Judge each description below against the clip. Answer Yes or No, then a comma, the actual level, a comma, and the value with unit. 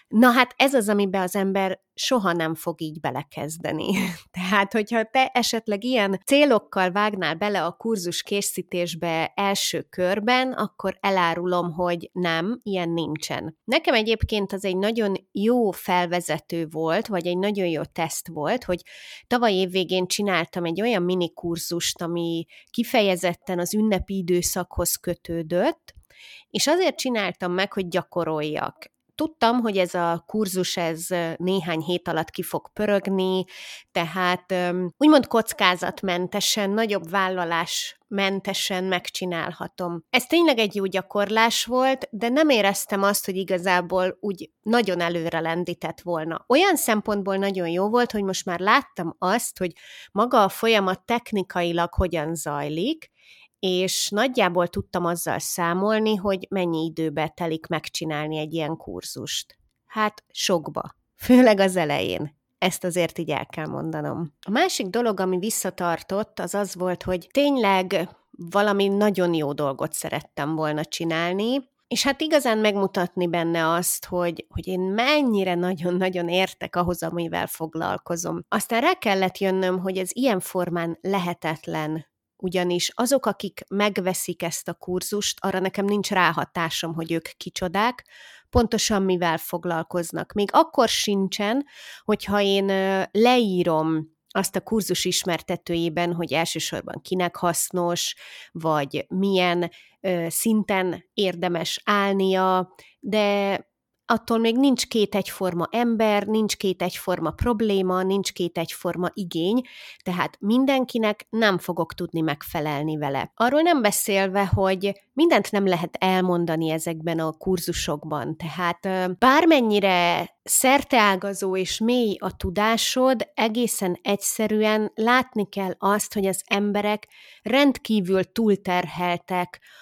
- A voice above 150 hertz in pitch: Yes, high, 190 Hz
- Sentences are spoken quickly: No, average, 125 wpm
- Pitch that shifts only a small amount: No, average, 3.6 semitones